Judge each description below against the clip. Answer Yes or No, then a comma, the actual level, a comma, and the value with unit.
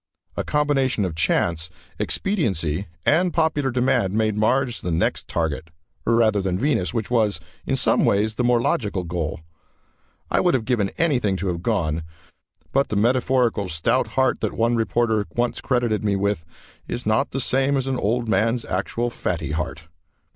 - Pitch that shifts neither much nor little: Yes, average, 5.0 semitones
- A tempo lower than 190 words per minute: Yes, average, 165 wpm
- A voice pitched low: Yes, low, 110 Hz